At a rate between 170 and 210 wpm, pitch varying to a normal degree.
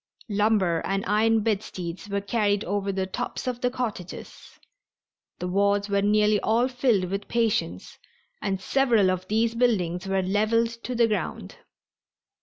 No: average, 145 wpm; average, 3.0 semitones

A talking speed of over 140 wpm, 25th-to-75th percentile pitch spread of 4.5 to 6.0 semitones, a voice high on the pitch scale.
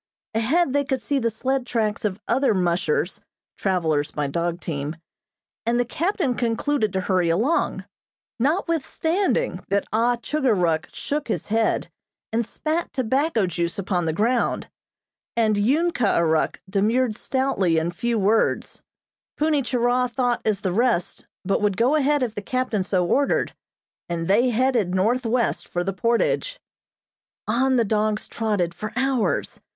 Yes: average, 150 wpm; wide, 5.6 semitones; high, 225 Hz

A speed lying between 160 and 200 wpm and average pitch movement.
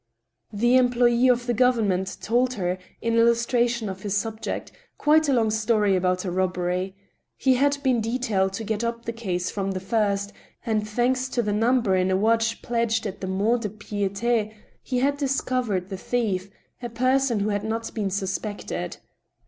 Yes: average, 175 wpm; average, 3.5 semitones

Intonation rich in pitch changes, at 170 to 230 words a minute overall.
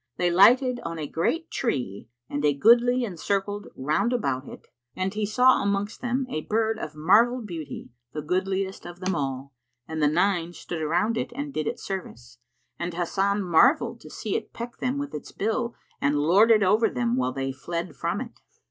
Yes: wide, 6.6 semitones; average, 190 wpm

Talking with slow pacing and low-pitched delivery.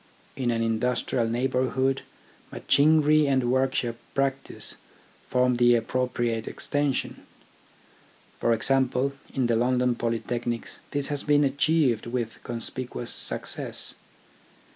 Yes: slow, 100 wpm; low, 125 Hz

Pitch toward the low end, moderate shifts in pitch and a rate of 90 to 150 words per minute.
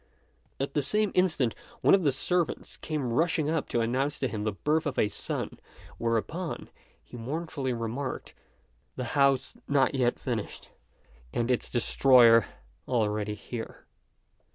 Yes: low, 130 Hz; average, 4.4 semitones; average, 140 wpm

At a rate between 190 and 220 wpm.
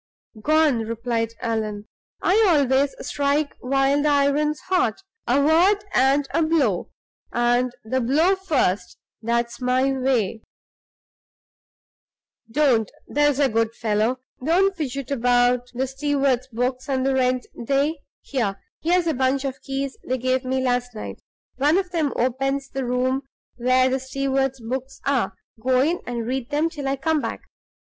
No: average, 145 wpm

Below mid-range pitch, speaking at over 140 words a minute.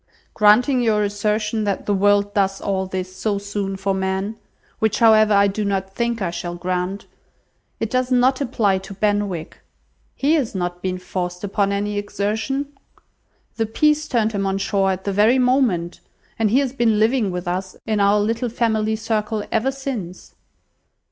No: high, 205 Hz; average, 170 wpm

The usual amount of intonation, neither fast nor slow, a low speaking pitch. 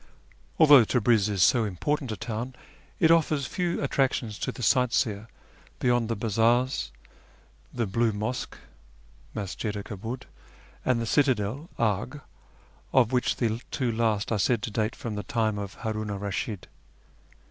Yes: average, 3.3 semitones; average, 160 wpm; low, 115 Hz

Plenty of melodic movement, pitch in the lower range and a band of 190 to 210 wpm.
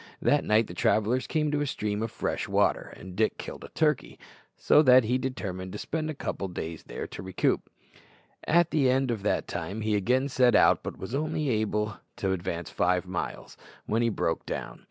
Yes: wide, 5.7 semitones; low, 110 Hz; fast, 205 wpm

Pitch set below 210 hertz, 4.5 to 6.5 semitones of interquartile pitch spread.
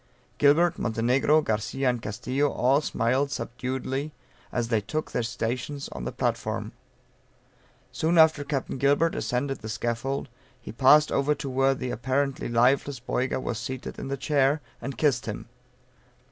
No: low, 135 Hz; average, 2.8 semitones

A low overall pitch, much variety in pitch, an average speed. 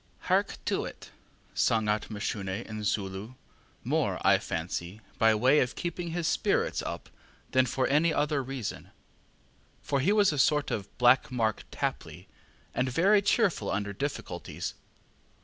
Yes: low, 125 Hz; wide, 6.0 semitones; average, 145 wpm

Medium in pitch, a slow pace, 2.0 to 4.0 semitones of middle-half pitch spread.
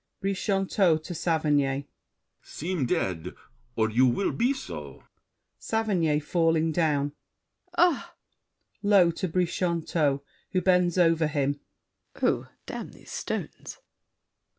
No: medium, 165 Hz; slow, 105 wpm; average, 4.4 semitones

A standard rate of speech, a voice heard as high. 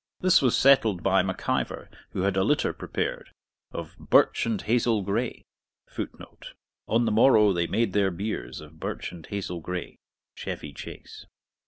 No: average, 160 wpm; low, 100 Hz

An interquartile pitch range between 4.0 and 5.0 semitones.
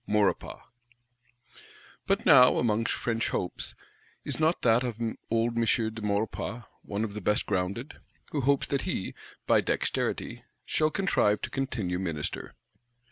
No: average, 3.5 semitones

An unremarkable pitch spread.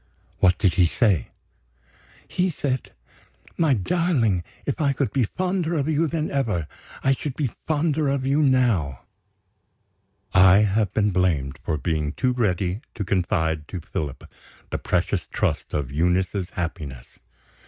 No: wide, 8.3 semitones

